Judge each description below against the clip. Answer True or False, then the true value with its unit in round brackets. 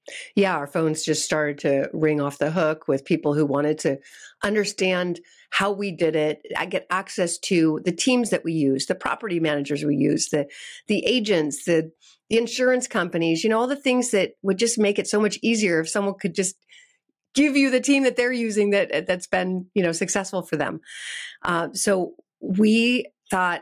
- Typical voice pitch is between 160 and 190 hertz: True (185 Hz)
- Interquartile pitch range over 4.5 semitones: True (5.1 semitones)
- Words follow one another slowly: False (195 wpm)